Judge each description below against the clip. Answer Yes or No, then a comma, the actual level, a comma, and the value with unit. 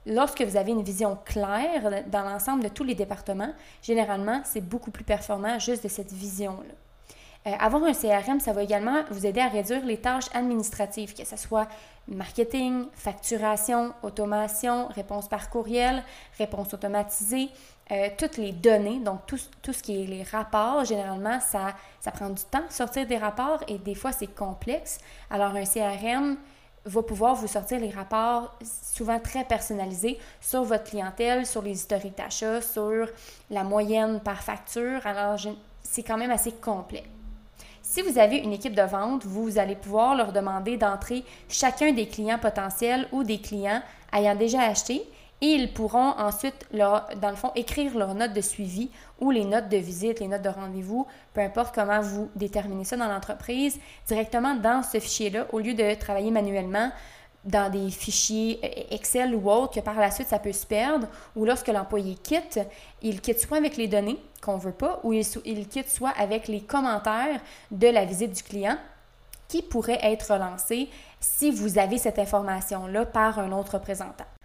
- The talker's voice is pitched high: Yes, high, 220 Hz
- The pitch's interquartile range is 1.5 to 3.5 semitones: Yes, average, 3.0 semitones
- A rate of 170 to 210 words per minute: Yes, average, 175 wpm